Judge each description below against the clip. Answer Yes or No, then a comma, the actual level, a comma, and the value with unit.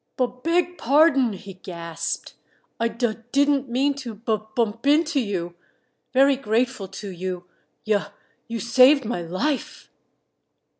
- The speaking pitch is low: No, high, 235 Hz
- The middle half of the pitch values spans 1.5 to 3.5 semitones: No, average, 5.2 semitones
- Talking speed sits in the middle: No, slow, 130 wpm